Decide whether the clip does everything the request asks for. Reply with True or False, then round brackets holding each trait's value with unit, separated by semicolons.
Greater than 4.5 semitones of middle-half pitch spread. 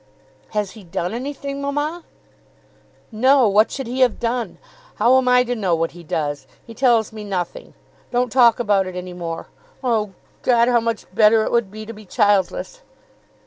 False (4.2 semitones)